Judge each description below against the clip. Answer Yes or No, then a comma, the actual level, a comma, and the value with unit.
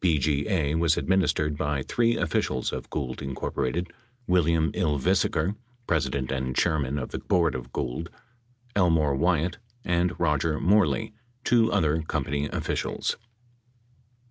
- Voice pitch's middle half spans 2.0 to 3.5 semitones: No, average, 3.9 semitones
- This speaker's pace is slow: Yes, slow, 115 wpm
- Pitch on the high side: No, very low, 80 Hz